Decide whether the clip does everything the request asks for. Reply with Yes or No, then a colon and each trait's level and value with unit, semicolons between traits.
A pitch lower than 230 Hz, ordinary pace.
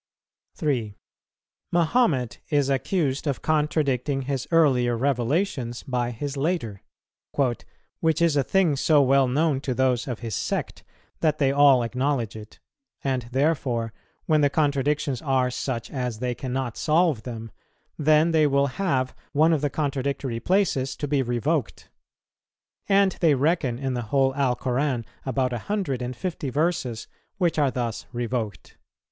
Yes: low, 135 Hz; average, 145 wpm